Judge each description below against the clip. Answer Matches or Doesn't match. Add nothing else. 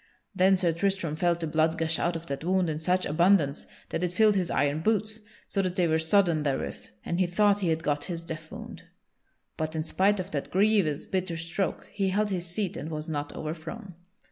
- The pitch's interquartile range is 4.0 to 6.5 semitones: Doesn't match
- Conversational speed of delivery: Doesn't match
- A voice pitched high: Doesn't match